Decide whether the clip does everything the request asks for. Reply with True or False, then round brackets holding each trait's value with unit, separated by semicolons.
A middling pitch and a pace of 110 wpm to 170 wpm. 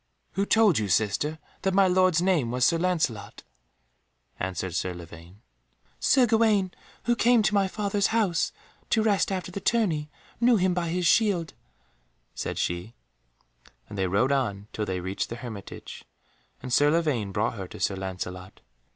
True (155 Hz; 160 wpm)